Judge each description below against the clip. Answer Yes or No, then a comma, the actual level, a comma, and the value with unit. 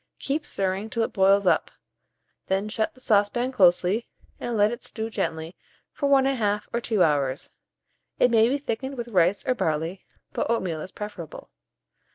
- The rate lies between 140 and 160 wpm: No, average, 170 wpm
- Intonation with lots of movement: No, average, 4.3 semitones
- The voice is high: Yes, high, 210 Hz